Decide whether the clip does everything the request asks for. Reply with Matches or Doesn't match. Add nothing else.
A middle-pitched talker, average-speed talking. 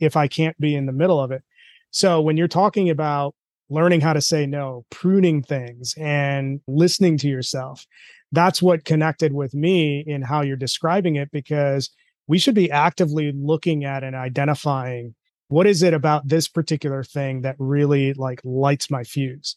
Matches